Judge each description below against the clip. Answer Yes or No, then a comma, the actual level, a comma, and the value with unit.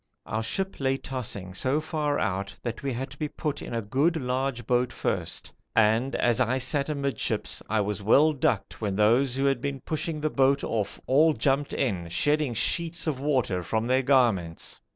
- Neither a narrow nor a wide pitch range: Yes, average, 4.4 semitones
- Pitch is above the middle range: No, low, 130 Hz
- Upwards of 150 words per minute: Yes, average, 190 wpm